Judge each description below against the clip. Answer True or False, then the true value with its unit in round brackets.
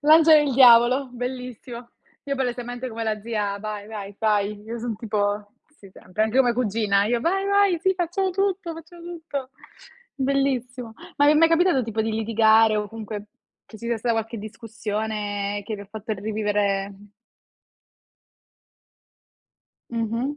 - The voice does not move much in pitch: False (4.3 semitones)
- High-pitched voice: True (230 Hz)